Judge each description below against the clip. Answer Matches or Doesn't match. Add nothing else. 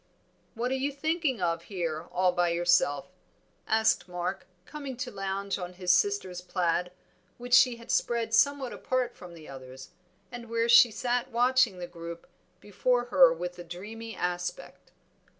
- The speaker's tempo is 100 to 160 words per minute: Matches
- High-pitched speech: Matches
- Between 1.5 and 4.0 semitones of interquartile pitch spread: Doesn't match